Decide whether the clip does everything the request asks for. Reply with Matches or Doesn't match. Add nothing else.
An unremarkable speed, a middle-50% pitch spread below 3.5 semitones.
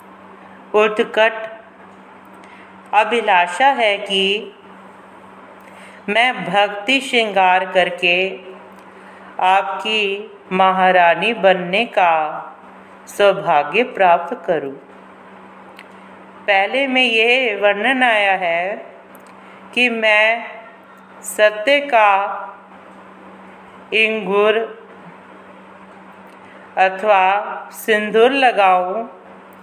Doesn't match